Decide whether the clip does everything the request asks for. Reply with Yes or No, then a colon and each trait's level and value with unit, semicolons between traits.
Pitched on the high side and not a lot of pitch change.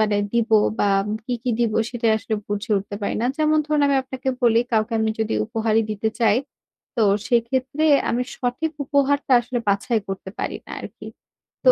No: high, 235 Hz; average, 3.1 semitones